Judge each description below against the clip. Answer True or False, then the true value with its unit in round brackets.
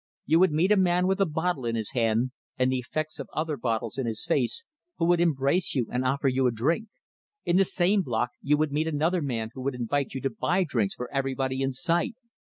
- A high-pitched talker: False (140 Hz)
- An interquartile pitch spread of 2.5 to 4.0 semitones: False (5.3 semitones)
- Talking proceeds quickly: True (235 wpm)